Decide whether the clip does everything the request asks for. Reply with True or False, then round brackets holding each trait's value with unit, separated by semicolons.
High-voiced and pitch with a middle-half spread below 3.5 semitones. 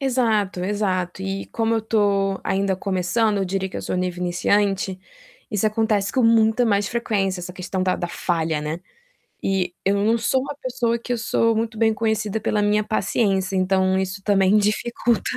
True (200 Hz; 2.9 semitones)